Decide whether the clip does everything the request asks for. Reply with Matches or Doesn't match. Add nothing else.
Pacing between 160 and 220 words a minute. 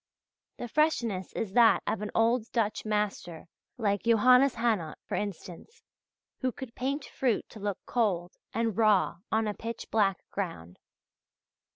Doesn't match